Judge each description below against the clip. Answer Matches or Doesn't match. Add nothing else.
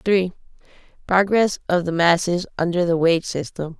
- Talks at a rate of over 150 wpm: Doesn't match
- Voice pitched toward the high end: Doesn't match